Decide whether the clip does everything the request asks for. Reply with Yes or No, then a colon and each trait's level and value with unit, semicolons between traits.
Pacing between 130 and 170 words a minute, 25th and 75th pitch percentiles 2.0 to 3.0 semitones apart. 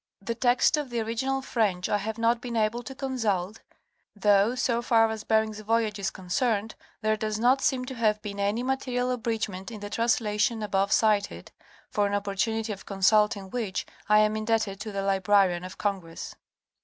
No: average, 180 wpm; narrow, 2.5 semitones